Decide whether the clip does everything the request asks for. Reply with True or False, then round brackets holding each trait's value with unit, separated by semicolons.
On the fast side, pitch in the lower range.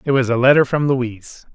True (235 wpm; 130 Hz)